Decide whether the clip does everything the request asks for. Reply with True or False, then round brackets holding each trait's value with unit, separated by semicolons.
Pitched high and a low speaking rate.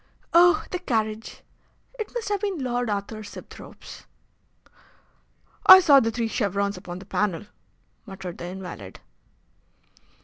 True (220 Hz; 125 wpm)